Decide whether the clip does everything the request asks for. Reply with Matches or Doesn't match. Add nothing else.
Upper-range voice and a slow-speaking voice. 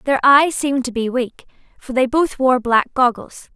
Doesn't match